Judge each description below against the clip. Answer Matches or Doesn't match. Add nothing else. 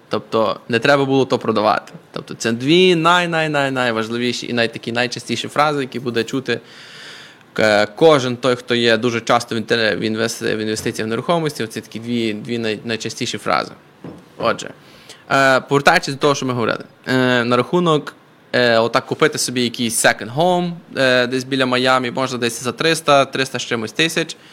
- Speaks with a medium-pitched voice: Doesn't match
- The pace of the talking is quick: Doesn't match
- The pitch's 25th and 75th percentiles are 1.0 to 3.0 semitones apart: Doesn't match